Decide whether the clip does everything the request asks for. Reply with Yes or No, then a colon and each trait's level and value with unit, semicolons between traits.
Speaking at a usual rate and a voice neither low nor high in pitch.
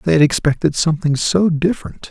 Yes: average, 170 wpm; medium, 150 Hz